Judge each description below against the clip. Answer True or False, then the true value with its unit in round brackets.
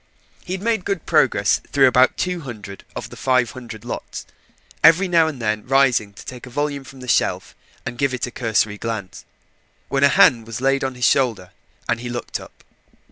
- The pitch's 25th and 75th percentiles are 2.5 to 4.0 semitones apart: True (3.5 semitones)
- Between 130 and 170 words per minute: False (200 wpm)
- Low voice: True (125 Hz)